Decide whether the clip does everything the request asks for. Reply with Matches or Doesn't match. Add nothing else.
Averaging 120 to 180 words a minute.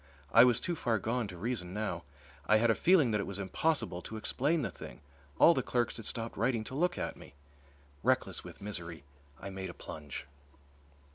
Doesn't match